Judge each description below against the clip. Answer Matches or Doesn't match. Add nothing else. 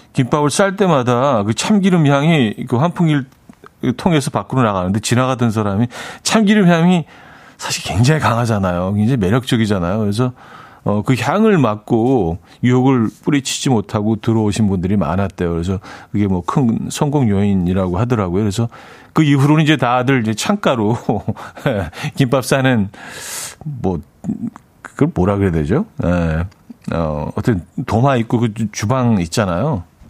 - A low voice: Matches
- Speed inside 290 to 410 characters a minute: Matches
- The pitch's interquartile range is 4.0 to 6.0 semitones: Matches